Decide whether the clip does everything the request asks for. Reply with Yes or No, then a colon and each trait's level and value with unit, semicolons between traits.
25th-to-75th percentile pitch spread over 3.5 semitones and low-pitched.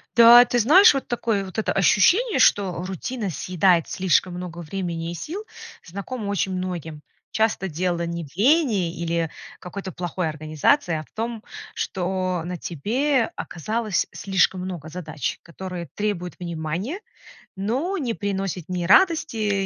No: average, 4.8 semitones; medium, 185 Hz